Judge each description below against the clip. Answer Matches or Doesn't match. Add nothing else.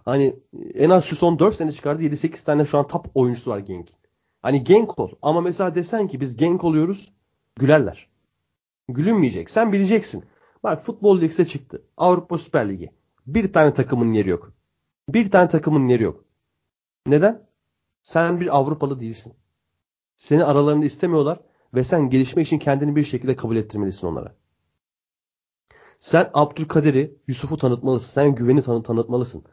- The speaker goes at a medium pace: Doesn't match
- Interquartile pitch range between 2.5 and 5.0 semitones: Doesn't match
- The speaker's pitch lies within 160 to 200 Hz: Doesn't match